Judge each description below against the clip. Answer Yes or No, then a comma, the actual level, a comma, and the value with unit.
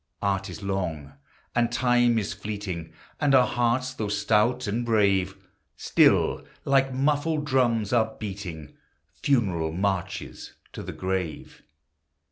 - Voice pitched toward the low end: Yes, low, 105 Hz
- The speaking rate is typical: No, slow, 120 wpm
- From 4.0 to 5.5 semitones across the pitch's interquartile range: Yes, average, 4.4 semitones